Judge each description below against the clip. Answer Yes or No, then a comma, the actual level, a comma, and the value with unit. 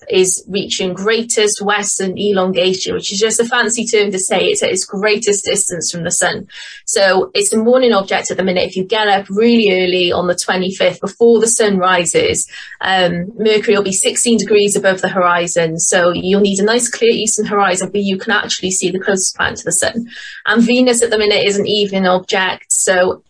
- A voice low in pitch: No, high, 205 Hz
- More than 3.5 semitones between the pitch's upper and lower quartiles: No, average, 3.1 semitones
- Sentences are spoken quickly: Yes, fast, 210 wpm